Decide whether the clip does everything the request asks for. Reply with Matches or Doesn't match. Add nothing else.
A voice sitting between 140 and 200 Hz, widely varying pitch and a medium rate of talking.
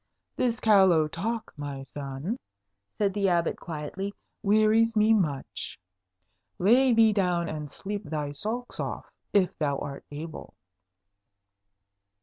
Doesn't match